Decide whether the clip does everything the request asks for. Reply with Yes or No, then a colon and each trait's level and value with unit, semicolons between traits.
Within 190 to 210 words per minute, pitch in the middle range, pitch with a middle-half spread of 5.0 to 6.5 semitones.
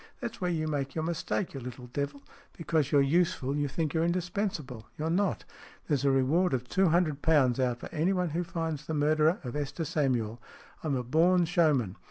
No: average, 200 wpm; medium, 155 Hz; average, 4.0 semitones